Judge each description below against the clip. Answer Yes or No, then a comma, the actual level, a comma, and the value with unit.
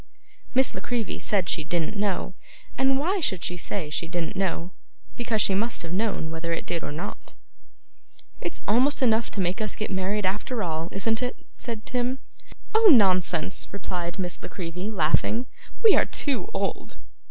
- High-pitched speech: Yes, high, 200 Hz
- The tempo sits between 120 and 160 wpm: No, average, 175 wpm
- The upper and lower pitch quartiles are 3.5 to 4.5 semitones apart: No, average, 5.3 semitones